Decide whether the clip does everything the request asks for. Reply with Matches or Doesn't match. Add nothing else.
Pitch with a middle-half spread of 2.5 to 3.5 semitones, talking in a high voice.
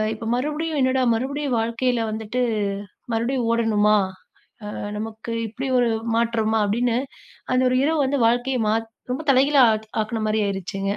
Matches